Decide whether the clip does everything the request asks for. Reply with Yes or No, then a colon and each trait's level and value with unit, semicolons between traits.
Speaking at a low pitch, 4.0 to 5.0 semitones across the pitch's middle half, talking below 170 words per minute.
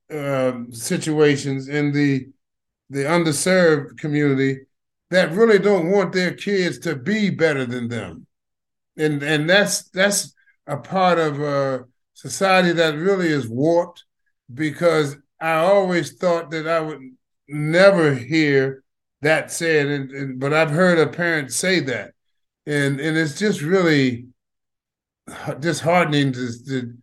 No: medium, 155 Hz; average, 4.3 semitones; slow, 135 wpm